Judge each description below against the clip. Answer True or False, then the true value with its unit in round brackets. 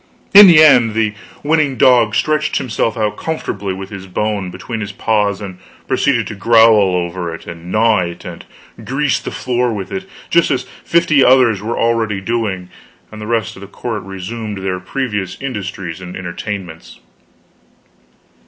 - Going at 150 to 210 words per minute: True (160 wpm)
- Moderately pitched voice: False (110 Hz)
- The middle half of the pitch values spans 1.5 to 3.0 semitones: False (4.4 semitones)